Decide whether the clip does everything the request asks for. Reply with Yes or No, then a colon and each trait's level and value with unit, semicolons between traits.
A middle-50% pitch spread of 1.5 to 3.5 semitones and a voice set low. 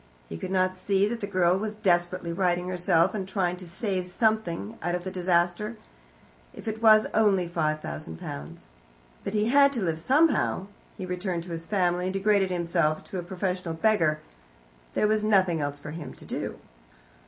No: average, 3.2 semitones; medium, 185 Hz